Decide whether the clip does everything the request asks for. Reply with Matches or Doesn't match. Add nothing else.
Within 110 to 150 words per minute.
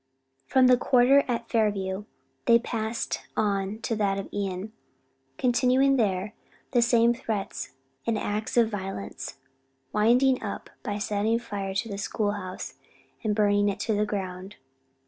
Matches